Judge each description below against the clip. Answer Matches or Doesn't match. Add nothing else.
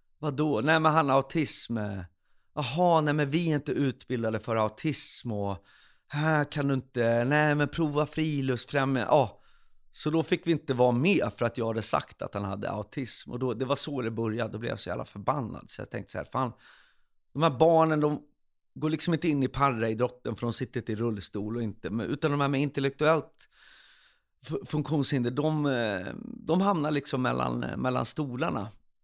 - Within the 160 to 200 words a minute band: Matches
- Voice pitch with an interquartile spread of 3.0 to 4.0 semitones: Doesn't match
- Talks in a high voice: Doesn't match